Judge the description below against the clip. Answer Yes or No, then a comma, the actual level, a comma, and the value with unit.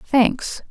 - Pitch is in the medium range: No, very high, 250 Hz